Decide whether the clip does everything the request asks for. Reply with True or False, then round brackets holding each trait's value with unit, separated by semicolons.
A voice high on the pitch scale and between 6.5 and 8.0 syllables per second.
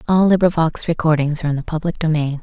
False (160 Hz; 6.8 syllables/s)